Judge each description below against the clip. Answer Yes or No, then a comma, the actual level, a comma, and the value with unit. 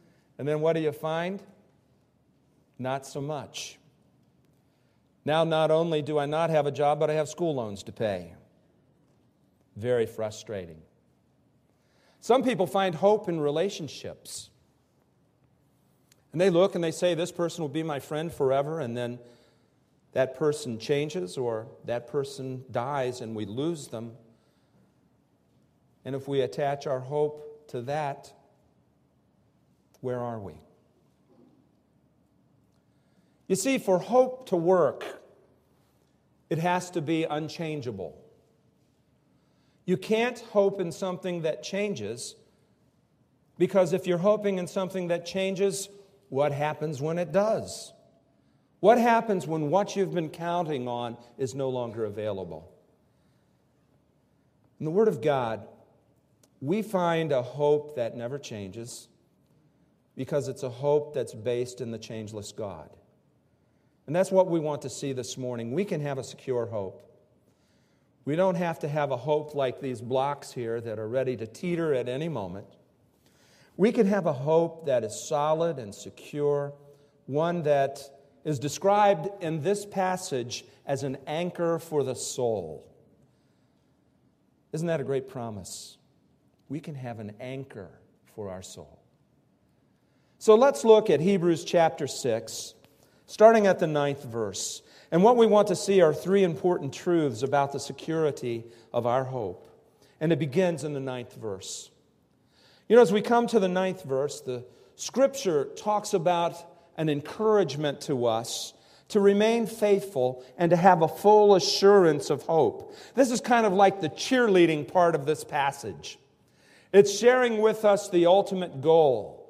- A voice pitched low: No, medium, 155 Hz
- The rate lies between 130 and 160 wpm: Yes, average, 145 wpm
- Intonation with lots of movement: Yes, wide, 6.0 semitones